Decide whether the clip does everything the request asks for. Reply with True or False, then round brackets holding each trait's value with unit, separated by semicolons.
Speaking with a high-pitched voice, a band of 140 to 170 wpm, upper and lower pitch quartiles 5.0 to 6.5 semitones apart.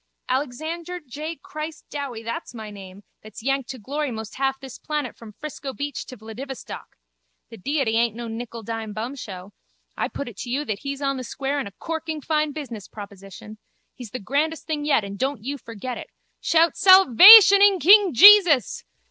False (270 Hz; 180 wpm; 5.3 semitones)